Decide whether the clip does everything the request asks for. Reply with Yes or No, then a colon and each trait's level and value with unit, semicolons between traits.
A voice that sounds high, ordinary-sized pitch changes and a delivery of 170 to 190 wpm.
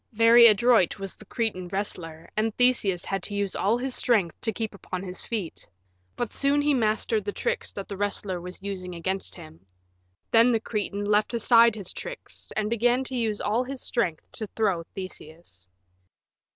Yes: high, 210 Hz; average, 3.8 semitones; average, 180 wpm